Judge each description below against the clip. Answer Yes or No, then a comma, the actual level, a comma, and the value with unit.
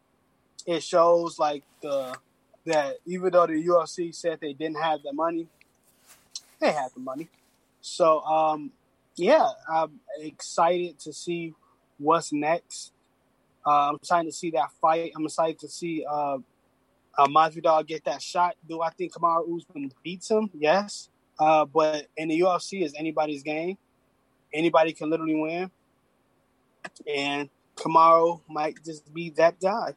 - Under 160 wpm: Yes, average, 150 wpm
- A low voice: No, medium, 160 Hz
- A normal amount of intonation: No, narrow, 2.3 semitones